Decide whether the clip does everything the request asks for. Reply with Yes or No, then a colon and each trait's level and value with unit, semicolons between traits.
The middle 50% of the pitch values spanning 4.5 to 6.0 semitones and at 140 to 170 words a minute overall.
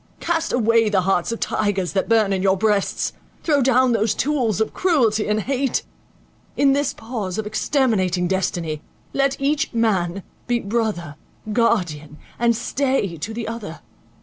Yes: average, 4.9 semitones; average, 150 wpm